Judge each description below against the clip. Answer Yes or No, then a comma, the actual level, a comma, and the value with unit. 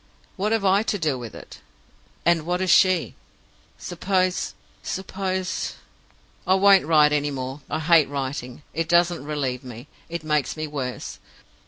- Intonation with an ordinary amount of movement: Yes, average, 4.5 semitones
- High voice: No, medium, 160 Hz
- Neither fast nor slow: Yes, average, 150 wpm